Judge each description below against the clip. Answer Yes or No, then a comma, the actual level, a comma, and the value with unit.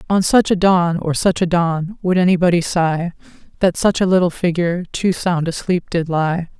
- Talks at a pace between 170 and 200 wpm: Yes, average, 190 wpm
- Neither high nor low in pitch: Yes, medium, 175 Hz